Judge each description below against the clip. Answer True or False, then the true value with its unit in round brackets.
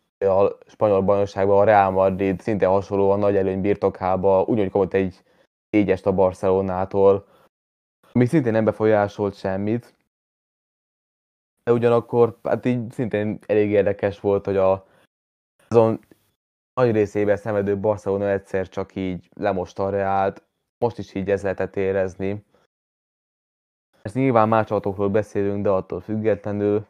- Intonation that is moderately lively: False (1.9 semitones)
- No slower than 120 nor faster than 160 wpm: True (125 wpm)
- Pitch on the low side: True (100 Hz)